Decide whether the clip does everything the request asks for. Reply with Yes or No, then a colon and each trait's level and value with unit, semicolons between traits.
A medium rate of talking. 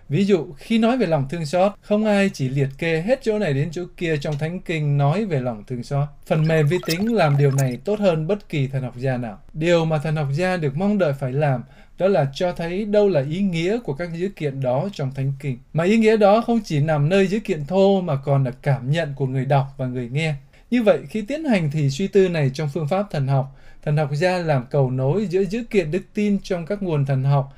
No: fast, 260 wpm